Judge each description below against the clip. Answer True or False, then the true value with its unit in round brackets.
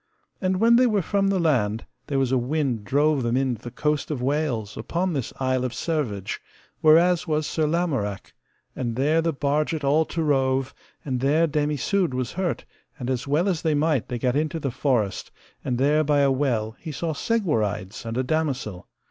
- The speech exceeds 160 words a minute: True (200 wpm)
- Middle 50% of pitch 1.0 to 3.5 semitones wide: False (4.2 semitones)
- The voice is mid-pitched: True (145 Hz)